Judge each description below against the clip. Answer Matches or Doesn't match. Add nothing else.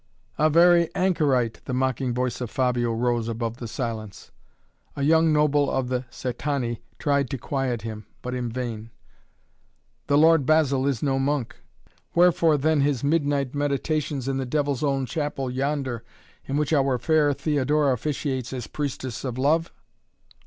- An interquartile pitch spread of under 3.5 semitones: Matches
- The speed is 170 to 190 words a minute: Doesn't match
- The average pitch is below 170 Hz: Matches